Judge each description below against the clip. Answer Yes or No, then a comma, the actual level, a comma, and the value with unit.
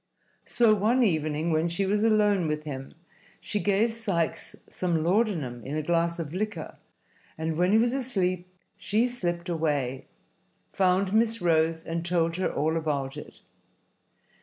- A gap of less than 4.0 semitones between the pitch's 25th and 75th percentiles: No, average, 4.7 semitones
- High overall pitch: No, medium, 175 Hz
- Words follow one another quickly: No, average, 150 wpm